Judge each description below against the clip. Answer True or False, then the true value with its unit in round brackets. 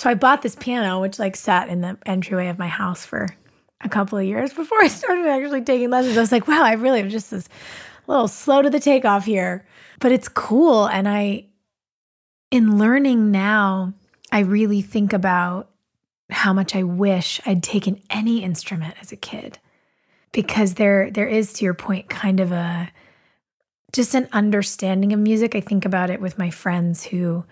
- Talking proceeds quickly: False (190 wpm)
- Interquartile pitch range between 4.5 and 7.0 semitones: False (3.7 semitones)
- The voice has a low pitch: False (205 Hz)